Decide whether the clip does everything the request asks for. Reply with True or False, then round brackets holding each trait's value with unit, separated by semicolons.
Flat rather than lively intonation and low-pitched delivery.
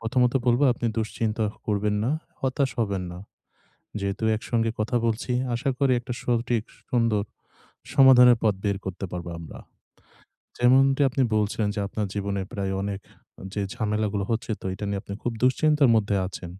False (3.4 semitones; 110 Hz)